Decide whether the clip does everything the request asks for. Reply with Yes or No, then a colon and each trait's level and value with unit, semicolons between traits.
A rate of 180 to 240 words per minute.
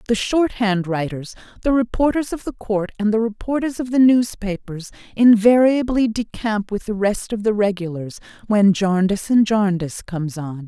No: average, 165 wpm